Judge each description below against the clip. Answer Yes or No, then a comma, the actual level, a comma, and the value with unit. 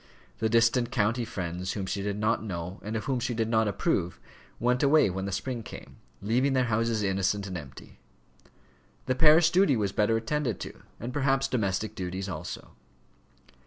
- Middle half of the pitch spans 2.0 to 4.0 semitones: No, average, 4.4 semitones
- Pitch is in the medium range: No, low, 110 Hz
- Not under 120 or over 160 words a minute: No, average, 175 wpm